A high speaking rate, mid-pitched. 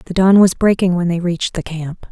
Yes: fast, 255 wpm; medium, 180 Hz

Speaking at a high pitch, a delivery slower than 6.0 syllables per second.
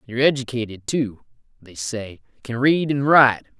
No: low, 120 Hz; 5.1 syllables/s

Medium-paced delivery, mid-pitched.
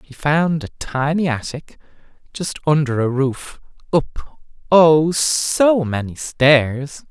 No: slow, 120 wpm; medium, 145 Hz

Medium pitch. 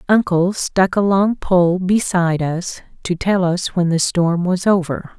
Yes: medium, 180 Hz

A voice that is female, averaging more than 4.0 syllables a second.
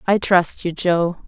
No: female; 3.5 syllables/s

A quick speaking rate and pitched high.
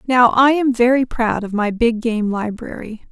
No: average, 195 wpm; high, 235 Hz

